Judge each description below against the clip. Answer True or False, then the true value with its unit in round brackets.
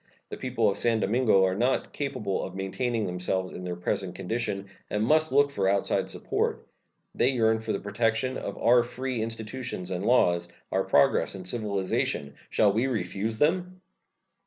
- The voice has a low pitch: True (110 Hz)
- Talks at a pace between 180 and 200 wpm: False (165 wpm)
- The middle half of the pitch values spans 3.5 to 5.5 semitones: True (4.4 semitones)